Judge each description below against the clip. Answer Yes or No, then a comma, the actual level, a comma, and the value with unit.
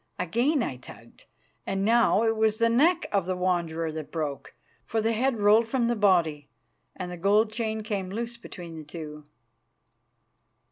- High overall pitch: Yes, high, 205 Hz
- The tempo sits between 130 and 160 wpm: No, average, 170 wpm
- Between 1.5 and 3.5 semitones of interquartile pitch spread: No, average, 5.3 semitones